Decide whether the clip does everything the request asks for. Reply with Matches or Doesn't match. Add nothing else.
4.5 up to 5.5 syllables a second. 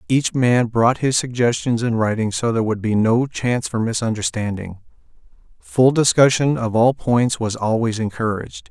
Matches